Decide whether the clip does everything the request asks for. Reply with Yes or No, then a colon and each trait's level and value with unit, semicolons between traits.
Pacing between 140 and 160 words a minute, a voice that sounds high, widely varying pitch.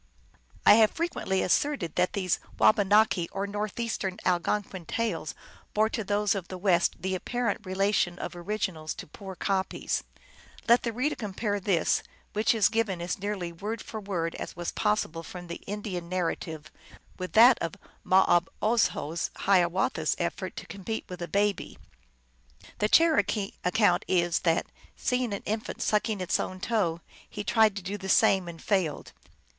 No: average, 155 wpm; high, 195 Hz; average, 3.2 semitones